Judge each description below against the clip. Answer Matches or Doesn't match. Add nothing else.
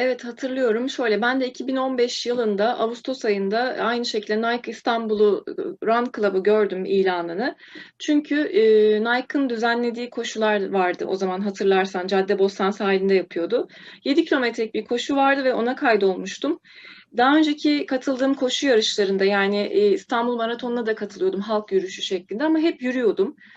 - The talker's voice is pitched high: Matches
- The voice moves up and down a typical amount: Matches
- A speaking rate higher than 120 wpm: Matches